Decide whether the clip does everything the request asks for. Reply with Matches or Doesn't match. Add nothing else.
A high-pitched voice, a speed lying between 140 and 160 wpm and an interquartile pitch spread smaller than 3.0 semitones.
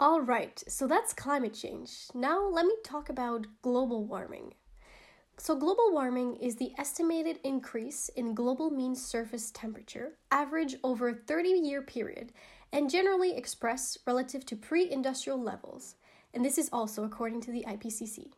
Doesn't match